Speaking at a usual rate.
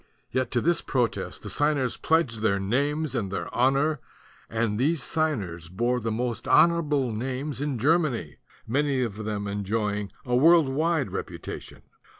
Yes: average, 150 wpm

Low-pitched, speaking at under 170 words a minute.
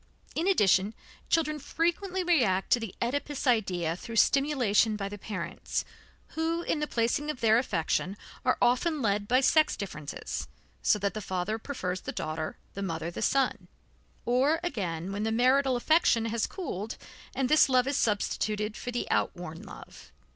No: high, 230 Hz; average, 160 wpm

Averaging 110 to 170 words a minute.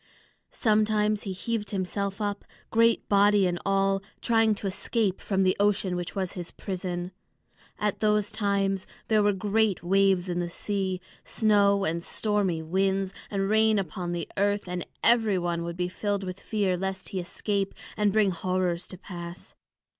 Yes: average, 160 wpm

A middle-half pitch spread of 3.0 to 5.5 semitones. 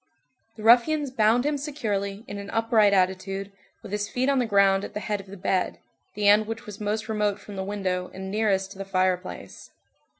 No: narrow, 2.4 semitones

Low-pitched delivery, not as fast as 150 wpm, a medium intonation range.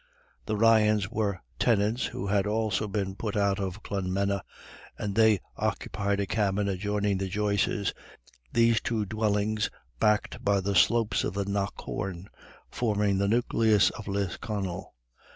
No: low, 100 Hz; slow, 135 wpm; narrow, 1.5 semitones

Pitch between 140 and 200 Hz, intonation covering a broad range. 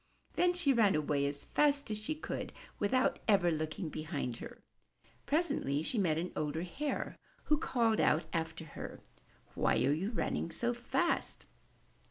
Yes: high, 190 Hz; wide, 8.8 semitones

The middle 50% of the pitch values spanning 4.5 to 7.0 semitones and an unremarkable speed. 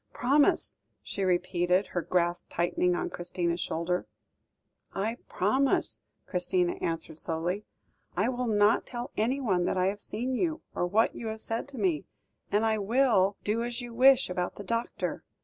Yes: average, 5.0 semitones; average, 160 wpm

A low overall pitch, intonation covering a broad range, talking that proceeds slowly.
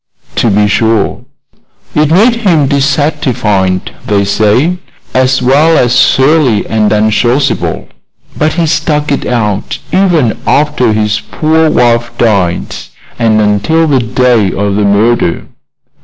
Yes: low, 125 Hz; wide, 6.0 semitones; slow, 125 wpm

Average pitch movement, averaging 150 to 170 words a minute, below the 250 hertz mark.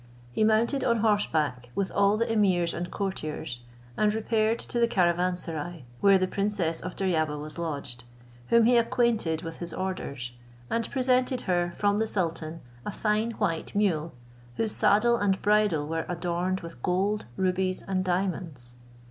Yes: average, 4.3 semitones; average, 155 wpm; medium, 185 Hz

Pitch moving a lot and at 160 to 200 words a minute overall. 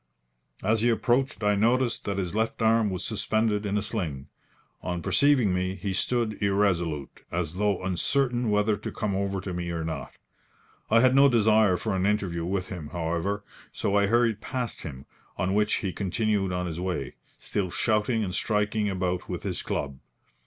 No: average, 3.3 semitones; average, 180 wpm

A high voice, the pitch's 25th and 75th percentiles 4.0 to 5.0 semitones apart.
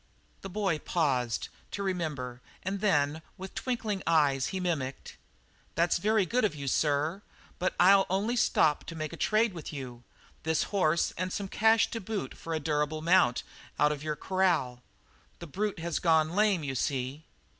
No: medium, 165 Hz; average, 4.7 semitones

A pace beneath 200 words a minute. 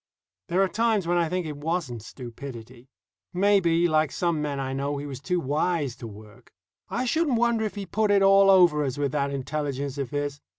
No: fast, 205 wpm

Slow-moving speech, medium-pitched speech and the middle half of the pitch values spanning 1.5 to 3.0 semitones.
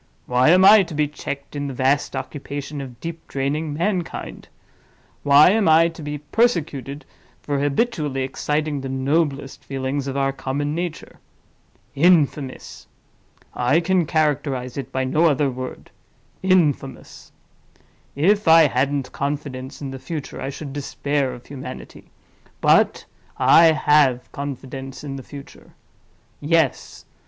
Yes: slow, 125 wpm; medium, 145 Hz; average, 2.7 semitones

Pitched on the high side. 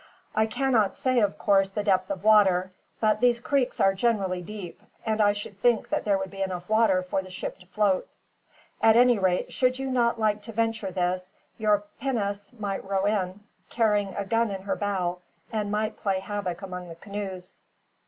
Yes: high, 205 Hz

